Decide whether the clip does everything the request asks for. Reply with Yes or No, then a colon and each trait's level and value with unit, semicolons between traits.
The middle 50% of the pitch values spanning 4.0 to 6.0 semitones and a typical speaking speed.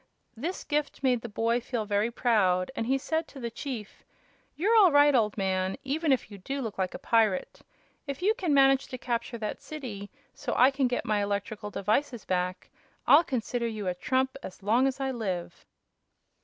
Yes: average, 4.8 semitones; average, 195 wpm